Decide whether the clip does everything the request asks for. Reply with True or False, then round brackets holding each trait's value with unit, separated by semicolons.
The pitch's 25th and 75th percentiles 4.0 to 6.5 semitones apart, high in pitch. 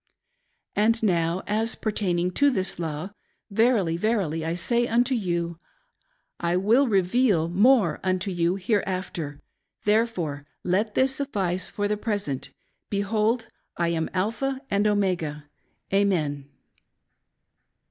True (4.5 semitones; 195 Hz)